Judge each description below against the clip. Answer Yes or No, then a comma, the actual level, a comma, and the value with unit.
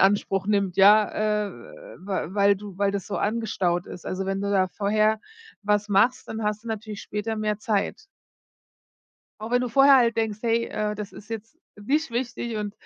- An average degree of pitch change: No, narrow, 1.9 semitones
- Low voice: No, high, 210 Hz